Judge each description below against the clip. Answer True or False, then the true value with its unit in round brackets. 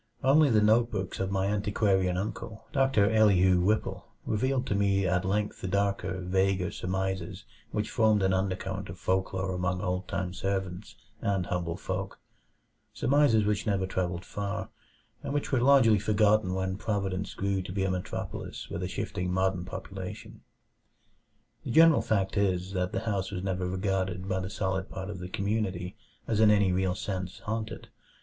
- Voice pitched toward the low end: True (95 Hz)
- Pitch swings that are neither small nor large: False (2.2 semitones)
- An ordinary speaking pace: True (165 wpm)